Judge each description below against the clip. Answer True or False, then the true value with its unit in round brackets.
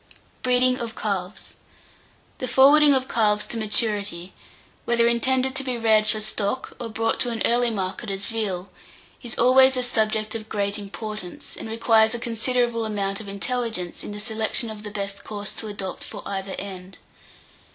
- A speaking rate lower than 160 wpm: False (170 wpm)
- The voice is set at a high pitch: True (220 Hz)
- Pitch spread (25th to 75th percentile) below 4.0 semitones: True (2.8 semitones)